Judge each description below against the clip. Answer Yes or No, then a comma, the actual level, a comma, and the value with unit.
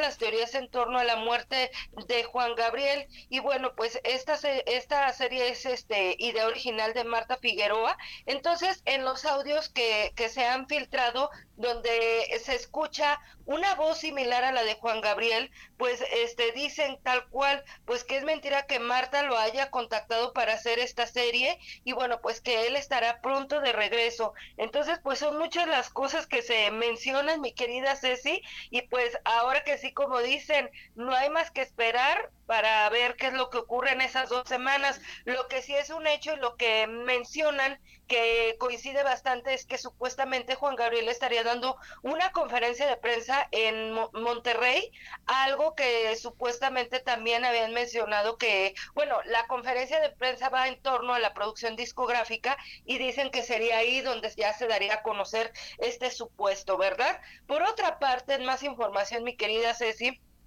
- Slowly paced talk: No, average, 170 wpm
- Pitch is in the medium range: No, very high, 250 Hz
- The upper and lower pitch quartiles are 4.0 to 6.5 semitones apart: No, average, 2.8 semitones